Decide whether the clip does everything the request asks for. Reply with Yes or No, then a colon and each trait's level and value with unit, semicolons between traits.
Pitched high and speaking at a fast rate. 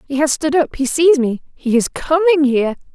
Yes: very high, 285 Hz; fast, 225 wpm